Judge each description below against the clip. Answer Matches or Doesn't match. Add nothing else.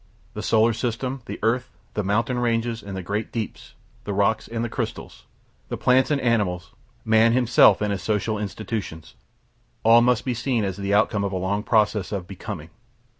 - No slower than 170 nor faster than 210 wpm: Matches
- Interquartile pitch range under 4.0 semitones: Matches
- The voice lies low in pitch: Matches